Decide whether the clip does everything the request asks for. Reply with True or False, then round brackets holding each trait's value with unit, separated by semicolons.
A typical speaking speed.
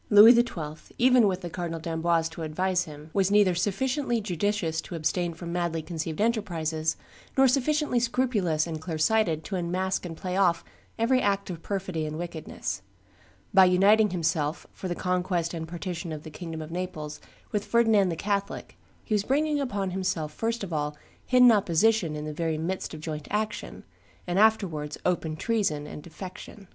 True (175 wpm)